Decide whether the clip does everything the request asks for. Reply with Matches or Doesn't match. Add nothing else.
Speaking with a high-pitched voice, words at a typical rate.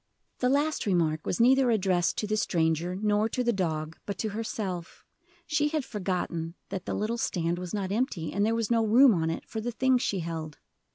Doesn't match